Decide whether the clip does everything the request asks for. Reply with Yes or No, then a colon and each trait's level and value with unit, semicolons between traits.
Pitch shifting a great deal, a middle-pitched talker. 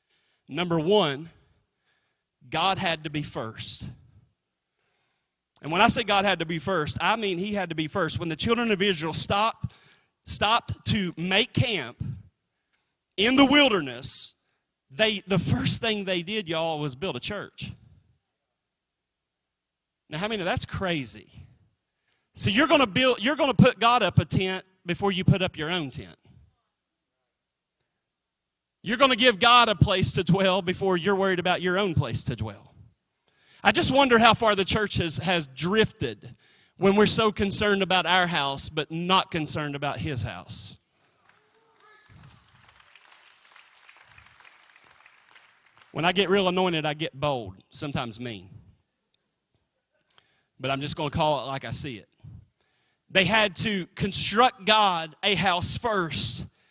Yes: wide, 6.2 semitones; medium, 180 Hz